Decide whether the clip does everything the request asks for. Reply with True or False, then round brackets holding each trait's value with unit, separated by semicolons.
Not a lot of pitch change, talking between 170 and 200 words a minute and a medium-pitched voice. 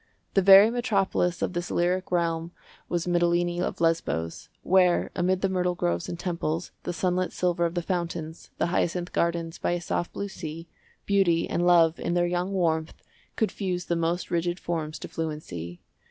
True (1.5 semitones; 175 wpm; 175 Hz)